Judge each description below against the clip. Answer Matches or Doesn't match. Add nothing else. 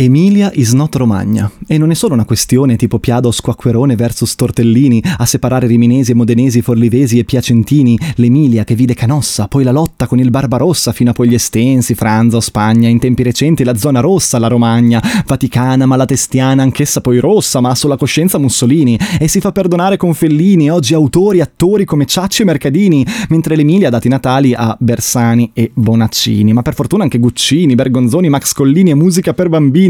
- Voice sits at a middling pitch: Doesn't match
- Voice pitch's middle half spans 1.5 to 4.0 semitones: Doesn't match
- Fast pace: Matches